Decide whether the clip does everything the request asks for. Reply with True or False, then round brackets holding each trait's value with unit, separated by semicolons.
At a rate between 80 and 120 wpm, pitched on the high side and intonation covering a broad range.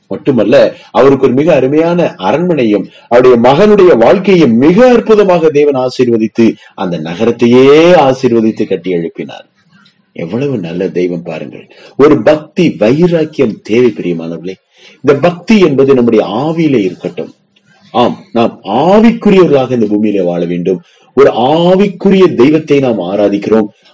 False (105 wpm; 130 Hz; 8.4 semitones)